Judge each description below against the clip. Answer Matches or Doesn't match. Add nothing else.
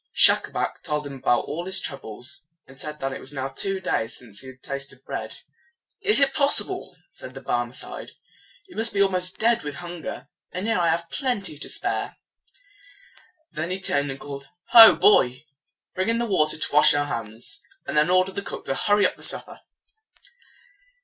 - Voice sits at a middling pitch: Matches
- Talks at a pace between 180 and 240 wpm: Matches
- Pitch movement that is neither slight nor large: Doesn't match